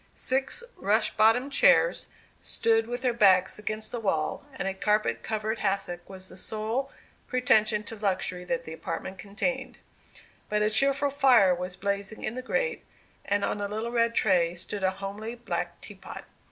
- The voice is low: No, high, 215 Hz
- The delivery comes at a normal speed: Yes, average, 165 wpm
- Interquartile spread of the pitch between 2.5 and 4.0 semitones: Yes, average, 3.7 semitones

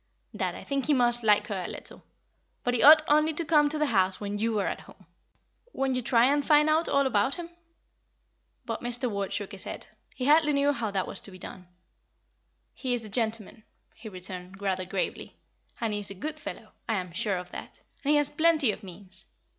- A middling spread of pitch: No, wide, 6.5 semitones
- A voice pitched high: Yes, high, 230 Hz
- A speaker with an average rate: No, fast, 220 wpm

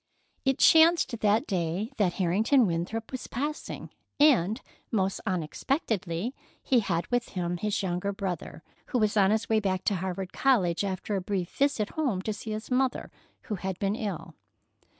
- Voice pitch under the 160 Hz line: No, high, 205 Hz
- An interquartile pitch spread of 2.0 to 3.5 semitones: No, average, 4.1 semitones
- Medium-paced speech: Yes, average, 165 wpm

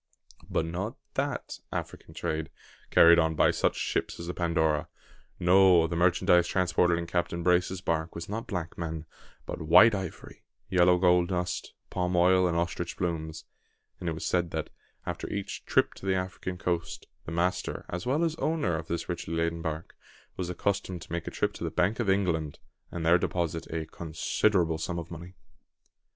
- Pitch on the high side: No, very low, 85 Hz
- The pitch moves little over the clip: Yes, narrow, 1.8 semitones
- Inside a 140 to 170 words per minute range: No, average, 180 wpm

